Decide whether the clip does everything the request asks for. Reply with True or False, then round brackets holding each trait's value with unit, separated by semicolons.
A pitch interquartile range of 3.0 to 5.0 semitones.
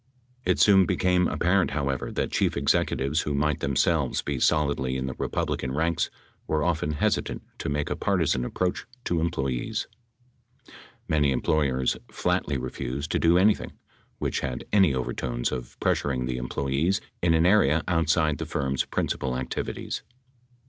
True (4.1 semitones)